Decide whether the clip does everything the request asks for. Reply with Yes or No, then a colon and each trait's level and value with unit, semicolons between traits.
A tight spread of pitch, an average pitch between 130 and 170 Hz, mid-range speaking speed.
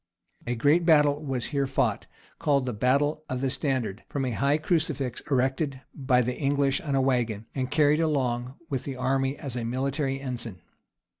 Yes: narrow, 2.3 semitones; low, 135 Hz; average, 175 wpm